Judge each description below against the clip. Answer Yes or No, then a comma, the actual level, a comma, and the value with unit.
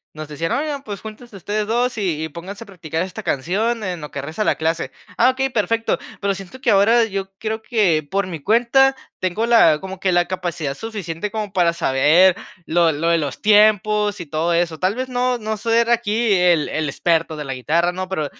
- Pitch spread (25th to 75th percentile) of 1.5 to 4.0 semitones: No, average, 5.0 semitones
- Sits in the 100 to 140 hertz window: No, high, 190 Hz